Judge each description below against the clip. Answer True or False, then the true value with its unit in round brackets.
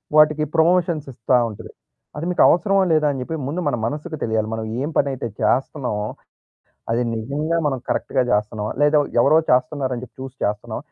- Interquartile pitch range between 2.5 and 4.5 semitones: False (4.9 semitones)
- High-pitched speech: False (135 Hz)